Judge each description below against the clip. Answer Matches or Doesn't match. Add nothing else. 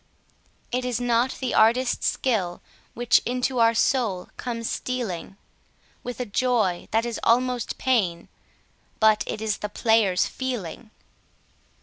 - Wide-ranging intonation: Doesn't match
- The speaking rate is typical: Doesn't match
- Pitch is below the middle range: Doesn't match